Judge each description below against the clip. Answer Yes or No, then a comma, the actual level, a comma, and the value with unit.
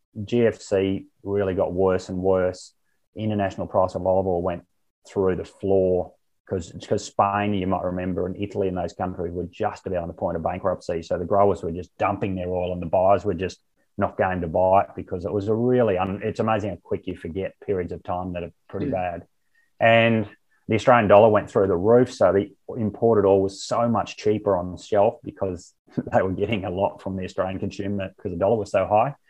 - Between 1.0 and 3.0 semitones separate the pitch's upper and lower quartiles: Yes, narrow, 2.4 semitones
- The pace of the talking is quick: Yes, fast, 215 wpm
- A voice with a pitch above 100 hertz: No, very low, 95 Hz